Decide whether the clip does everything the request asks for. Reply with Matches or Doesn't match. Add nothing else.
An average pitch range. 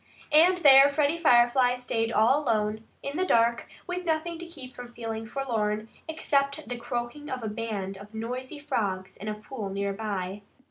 Matches